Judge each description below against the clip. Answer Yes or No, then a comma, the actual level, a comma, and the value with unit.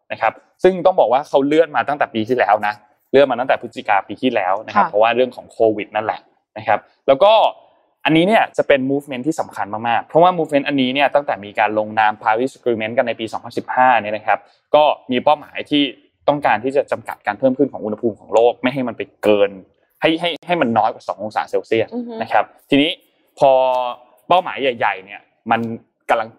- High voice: No, low, 130 Hz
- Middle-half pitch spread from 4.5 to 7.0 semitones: Yes, average, 5.0 semitones